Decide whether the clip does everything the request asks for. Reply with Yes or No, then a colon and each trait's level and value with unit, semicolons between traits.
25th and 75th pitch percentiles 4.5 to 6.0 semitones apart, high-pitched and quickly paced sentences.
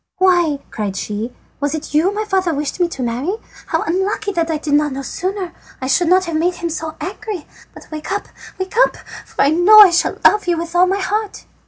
No: average, 4.1 semitones; very high, 345 Hz; fast, 225 wpm